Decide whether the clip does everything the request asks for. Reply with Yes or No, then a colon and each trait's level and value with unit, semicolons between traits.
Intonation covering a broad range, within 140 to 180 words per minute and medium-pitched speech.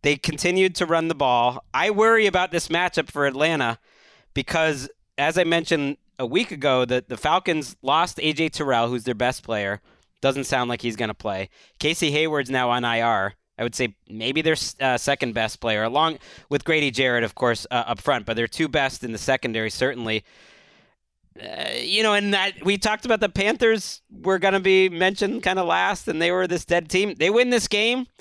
No: wide, 7.0 semitones; fast, 205 wpm; medium, 150 Hz